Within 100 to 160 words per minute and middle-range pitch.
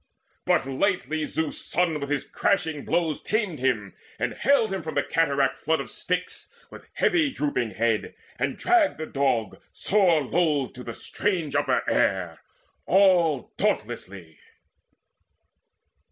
Yes: slow, 135 wpm; medium, 155 Hz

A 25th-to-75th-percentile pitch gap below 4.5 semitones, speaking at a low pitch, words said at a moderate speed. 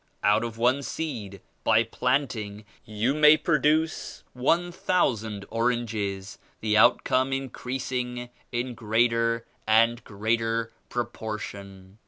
No: average, 3.0 semitones; low, 115 Hz; slow, 100 wpm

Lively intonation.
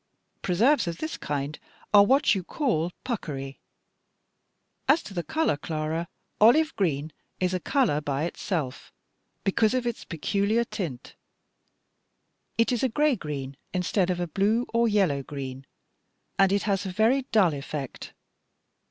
Yes: wide, 7.1 semitones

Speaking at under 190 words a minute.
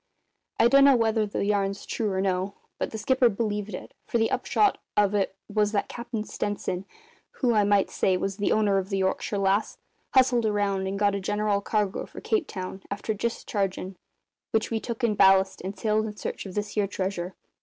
No: average, 195 wpm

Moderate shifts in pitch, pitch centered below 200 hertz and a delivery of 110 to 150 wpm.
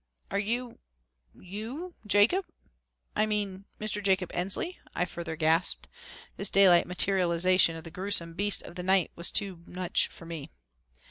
Yes: average, 3.1 semitones; high, 190 Hz; average, 145 wpm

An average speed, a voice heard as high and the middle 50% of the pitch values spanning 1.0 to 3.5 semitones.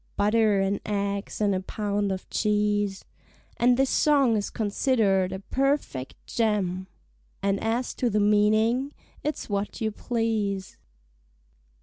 No: slow, 125 wpm; high, 210 Hz; narrow, 2.4 semitones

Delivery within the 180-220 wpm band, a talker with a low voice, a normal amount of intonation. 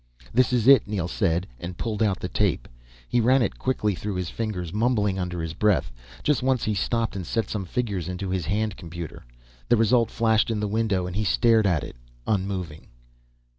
Yes: average, 200 wpm; low, 105 Hz; average, 4.0 semitones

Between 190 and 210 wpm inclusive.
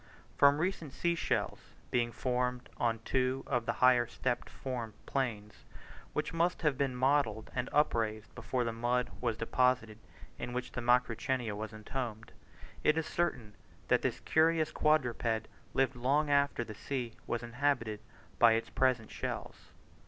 No: average, 150 wpm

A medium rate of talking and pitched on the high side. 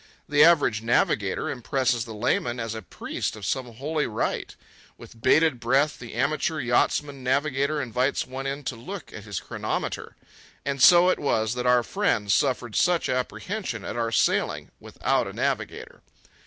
No: average, 160 wpm; low, 130 Hz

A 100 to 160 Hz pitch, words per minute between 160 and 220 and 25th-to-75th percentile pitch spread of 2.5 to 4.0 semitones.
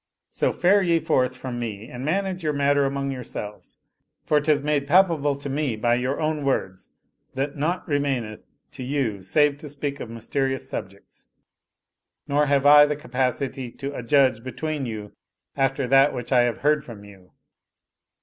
Yes: medium, 140 Hz; average, 170 wpm; average, 3.3 semitones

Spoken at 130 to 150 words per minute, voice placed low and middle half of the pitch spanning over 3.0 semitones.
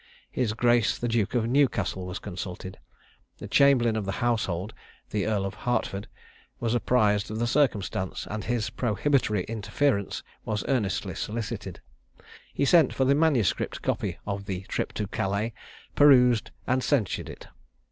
Yes: average, 145 wpm; low, 110 Hz; average, 3.7 semitones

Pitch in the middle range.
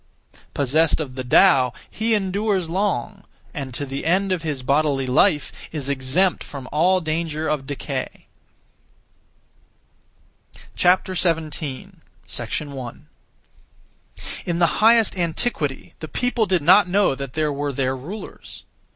Yes: medium, 155 Hz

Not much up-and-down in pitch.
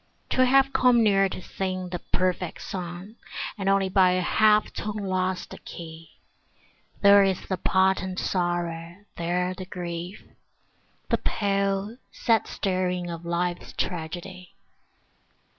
Yes: narrow, 2.0 semitones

